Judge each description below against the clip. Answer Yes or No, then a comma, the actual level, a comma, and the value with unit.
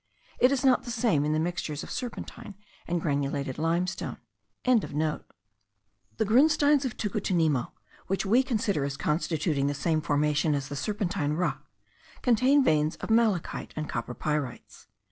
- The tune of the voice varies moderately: No, wide, 7.4 semitones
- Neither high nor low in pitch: Yes, medium, 165 Hz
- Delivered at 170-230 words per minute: No, average, 145 wpm